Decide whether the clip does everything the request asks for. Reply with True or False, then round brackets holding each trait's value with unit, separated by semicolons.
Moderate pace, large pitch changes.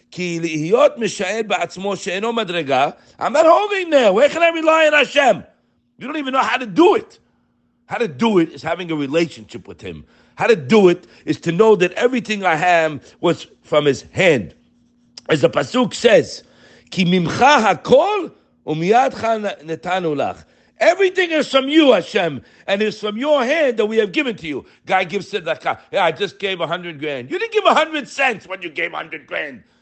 True (165 wpm; 8.5 semitones)